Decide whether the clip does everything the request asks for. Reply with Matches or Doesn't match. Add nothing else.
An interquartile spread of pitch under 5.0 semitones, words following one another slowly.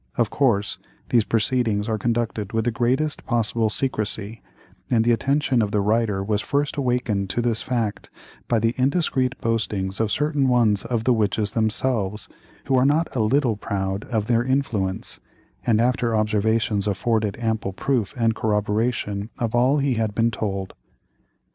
Doesn't match